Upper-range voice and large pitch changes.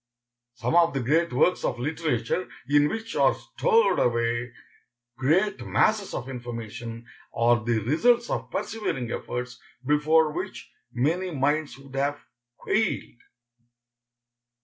No: medium, 140 Hz; wide, 5.8 semitones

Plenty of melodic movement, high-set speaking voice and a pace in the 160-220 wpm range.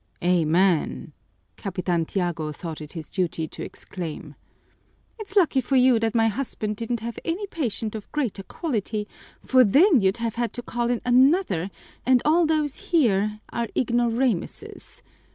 No: wide, 5.7 semitones; high, 230 Hz; average, 150 wpm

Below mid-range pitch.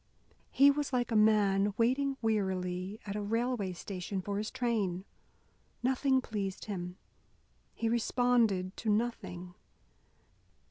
No: high, 210 Hz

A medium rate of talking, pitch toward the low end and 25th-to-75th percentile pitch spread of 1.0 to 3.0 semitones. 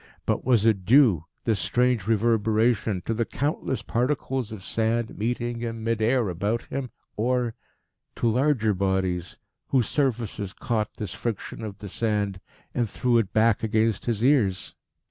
Yes: average, 150 wpm; low, 115 Hz; average, 2.7 semitones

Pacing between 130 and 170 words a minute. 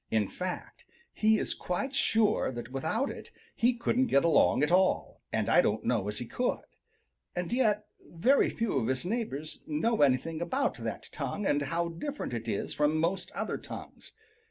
No: average, 180 wpm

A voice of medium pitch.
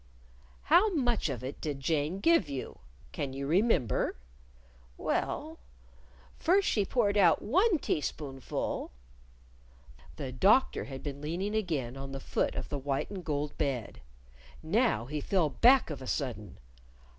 Yes: medium, 150 Hz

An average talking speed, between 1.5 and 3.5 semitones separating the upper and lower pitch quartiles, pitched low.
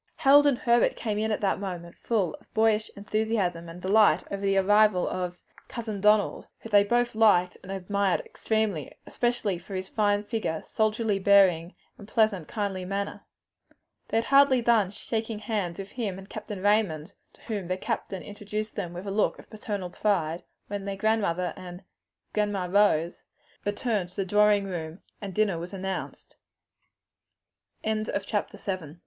No: average, 160 wpm; average, 2.7 semitones; high, 200 Hz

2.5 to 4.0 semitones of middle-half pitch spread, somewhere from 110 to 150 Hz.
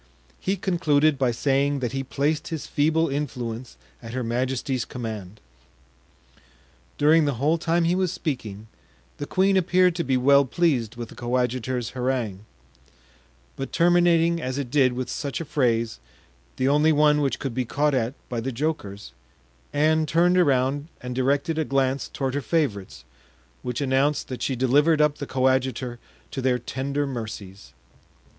Yes: average, 3.5 semitones; low, 135 Hz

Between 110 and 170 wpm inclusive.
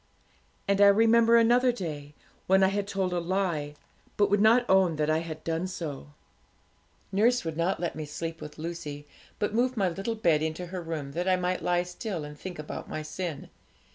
No: average, 200 wpm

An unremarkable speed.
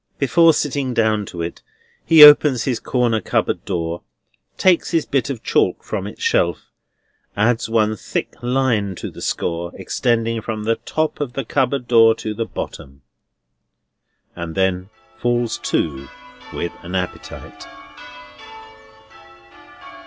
No: slow, 130 wpm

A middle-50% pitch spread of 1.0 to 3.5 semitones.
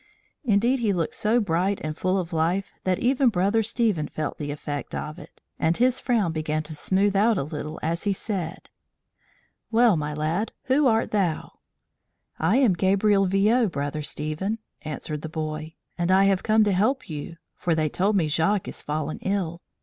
No: average, 5.2 semitones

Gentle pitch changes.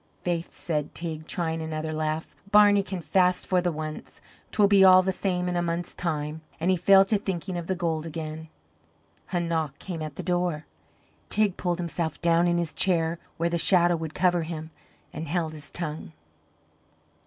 Yes: narrow, 2.3 semitones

